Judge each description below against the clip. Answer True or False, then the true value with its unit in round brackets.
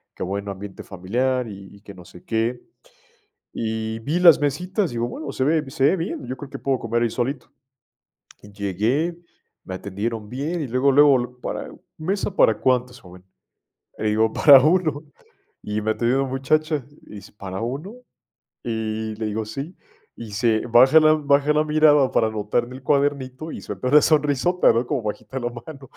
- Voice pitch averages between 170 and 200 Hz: False (125 Hz)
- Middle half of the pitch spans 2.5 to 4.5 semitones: False (4.9 semitones)